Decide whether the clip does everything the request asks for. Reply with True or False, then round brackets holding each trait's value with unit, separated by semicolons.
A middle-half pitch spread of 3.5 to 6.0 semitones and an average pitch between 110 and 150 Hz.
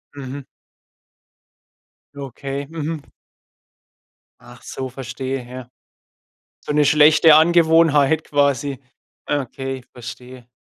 False (2.6 semitones; 140 Hz)